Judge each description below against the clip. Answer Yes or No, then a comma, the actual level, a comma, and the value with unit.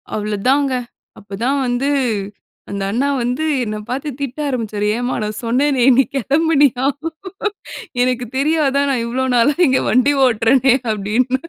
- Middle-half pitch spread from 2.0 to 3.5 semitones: Yes, average, 3.1 semitones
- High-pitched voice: Yes, very high, 255 Hz